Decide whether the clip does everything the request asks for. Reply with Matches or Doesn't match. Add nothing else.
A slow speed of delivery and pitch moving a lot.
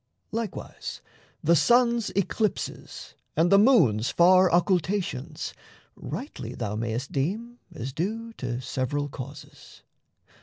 Matches